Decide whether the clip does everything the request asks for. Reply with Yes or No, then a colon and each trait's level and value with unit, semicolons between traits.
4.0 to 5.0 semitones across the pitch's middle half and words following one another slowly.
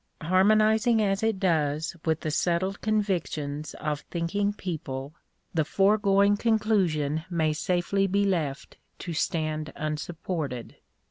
Yes: average, 4.6 semitones; slow, 115 wpm